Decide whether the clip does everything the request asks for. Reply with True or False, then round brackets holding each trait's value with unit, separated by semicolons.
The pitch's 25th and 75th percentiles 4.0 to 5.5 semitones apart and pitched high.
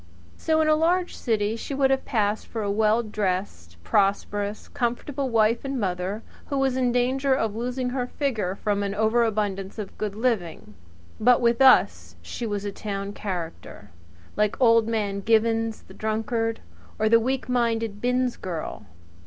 False (3.4 semitones; 220 Hz)